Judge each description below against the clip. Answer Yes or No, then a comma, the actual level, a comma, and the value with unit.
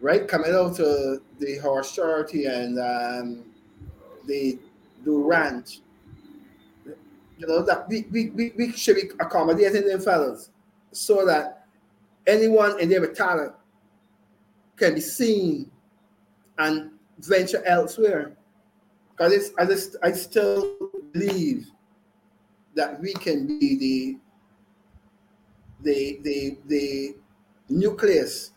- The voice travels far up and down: Yes, wide, 7.6 semitones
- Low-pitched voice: No, medium, 185 Hz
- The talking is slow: Yes, slow, 105 wpm